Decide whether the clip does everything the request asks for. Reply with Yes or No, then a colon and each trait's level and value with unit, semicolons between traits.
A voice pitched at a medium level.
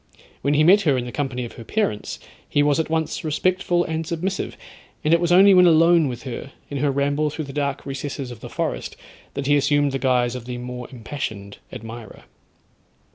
Yes: medium, 145 Hz